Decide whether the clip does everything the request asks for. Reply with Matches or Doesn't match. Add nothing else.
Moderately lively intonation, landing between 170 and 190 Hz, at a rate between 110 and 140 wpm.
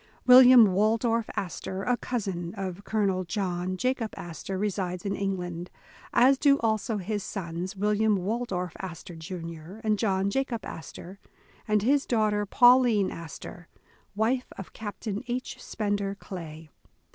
Doesn't match